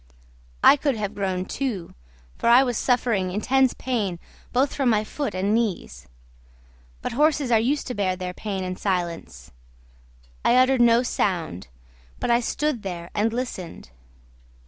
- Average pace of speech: Yes, average, 150 wpm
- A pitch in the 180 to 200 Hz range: No, high, 220 Hz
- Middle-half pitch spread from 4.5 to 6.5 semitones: Yes, wide, 5.4 semitones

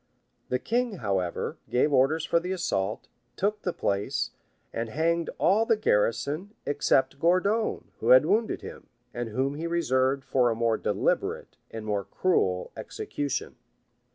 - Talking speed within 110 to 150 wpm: Yes, average, 145 wpm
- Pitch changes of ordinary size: No, wide, 7.7 semitones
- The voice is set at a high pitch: No, medium, 140 Hz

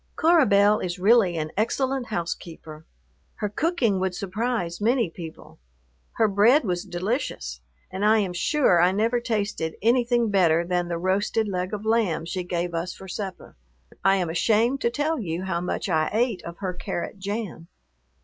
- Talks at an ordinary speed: Yes, average, 170 wpm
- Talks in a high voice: Yes, high, 195 Hz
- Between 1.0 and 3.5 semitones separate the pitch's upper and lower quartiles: No, average, 4.6 semitones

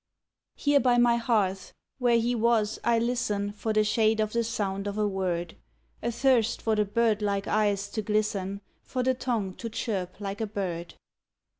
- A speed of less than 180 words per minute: Yes, average, 170 wpm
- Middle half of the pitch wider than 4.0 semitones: No, average, 2.8 semitones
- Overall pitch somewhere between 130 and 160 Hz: No, high, 215 Hz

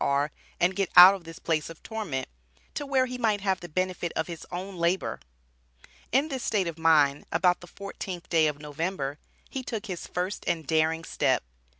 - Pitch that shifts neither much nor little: Yes, average, 3.5 semitones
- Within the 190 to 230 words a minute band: Yes, average, 195 wpm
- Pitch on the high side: No, medium, 175 Hz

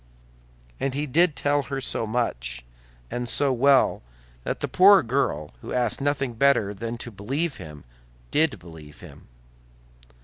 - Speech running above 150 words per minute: No, average, 145 wpm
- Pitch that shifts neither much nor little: No, wide, 5.7 semitones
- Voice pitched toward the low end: Yes, low, 125 Hz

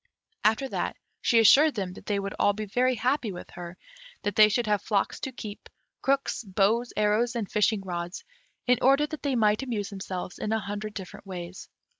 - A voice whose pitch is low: No, high, 210 Hz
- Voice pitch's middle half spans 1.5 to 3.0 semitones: No, average, 3.6 semitones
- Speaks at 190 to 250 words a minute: Yes, average, 195 wpm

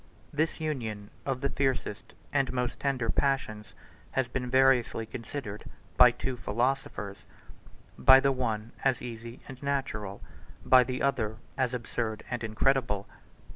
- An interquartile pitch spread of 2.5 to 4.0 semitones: Yes, average, 3.3 semitones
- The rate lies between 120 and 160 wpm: Yes, average, 140 wpm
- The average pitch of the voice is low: Yes, low, 125 Hz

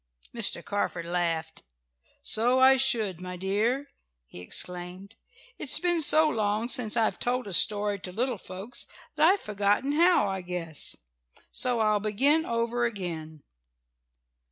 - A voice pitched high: Yes, high, 210 Hz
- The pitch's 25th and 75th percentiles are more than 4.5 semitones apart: Yes, wide, 5.4 semitones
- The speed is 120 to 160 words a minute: Yes, average, 140 wpm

